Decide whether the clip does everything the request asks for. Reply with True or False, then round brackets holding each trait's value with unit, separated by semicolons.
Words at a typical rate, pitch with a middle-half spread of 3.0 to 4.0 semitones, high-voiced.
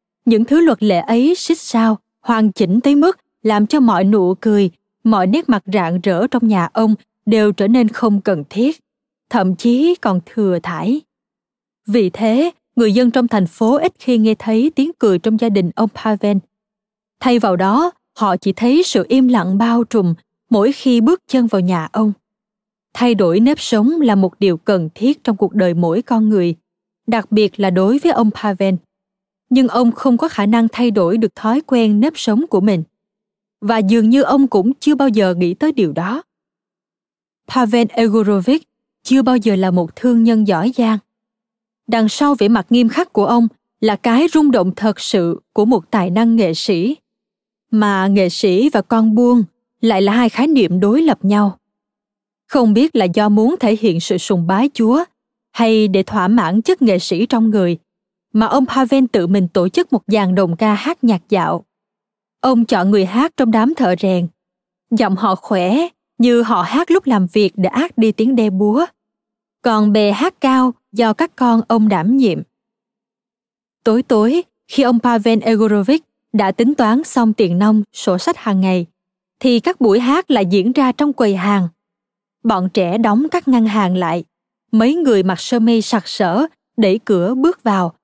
True (190 wpm; 3.6 semitones; 225 Hz)